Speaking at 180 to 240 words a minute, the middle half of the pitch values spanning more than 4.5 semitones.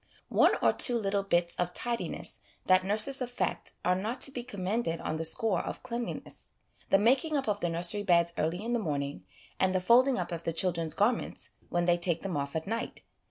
Yes: fast, 205 wpm; wide, 5.4 semitones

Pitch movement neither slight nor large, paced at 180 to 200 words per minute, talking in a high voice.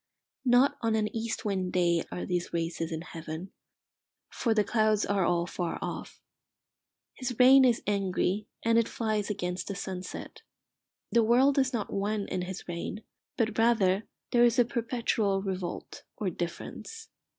No: average, 4.3 semitones; average, 155 wpm; high, 205 Hz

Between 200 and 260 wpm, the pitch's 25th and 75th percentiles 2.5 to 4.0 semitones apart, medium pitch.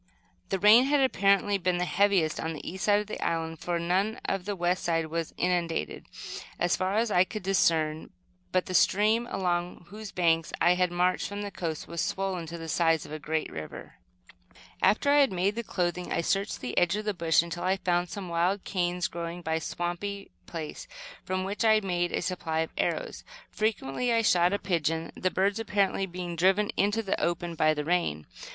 Yes: fast, 205 wpm; average, 3.0 semitones; medium, 180 Hz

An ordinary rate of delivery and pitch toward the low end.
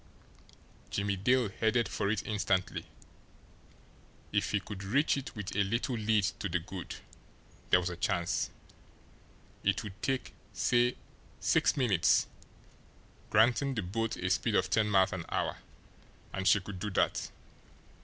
Yes: average, 145 wpm; low, 105 Hz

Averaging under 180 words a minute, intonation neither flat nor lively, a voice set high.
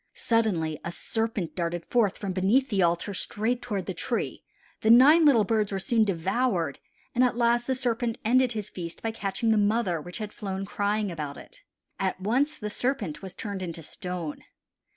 No: average, 185 wpm; average, 4.3 semitones; high, 210 Hz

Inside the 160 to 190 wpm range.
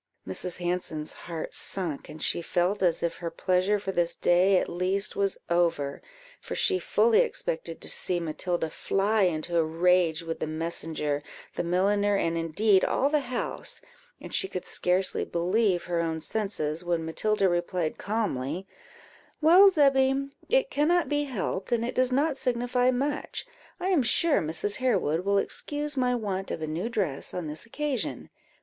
Yes: average, 165 wpm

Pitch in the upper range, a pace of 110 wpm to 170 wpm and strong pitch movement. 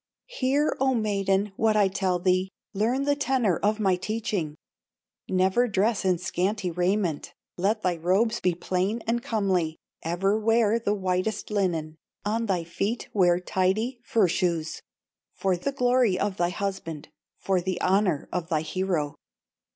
No: high, 195 Hz; average, 150 wpm; average, 3.4 semitones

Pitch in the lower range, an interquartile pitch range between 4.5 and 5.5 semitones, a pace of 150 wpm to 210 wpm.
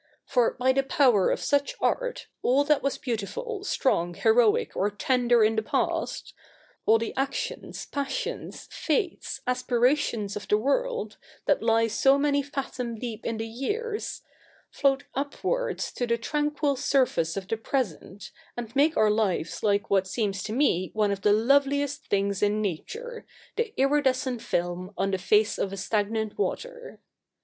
No: high, 240 Hz; average, 5.2 semitones; average, 160 wpm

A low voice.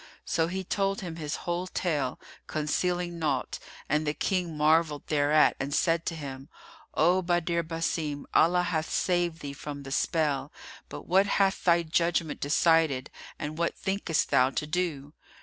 No: medium, 165 Hz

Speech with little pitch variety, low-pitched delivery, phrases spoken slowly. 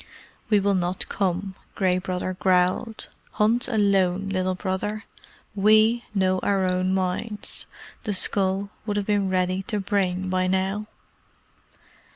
No: narrow, 1.9 semitones; high, 190 Hz; slow, 130 wpm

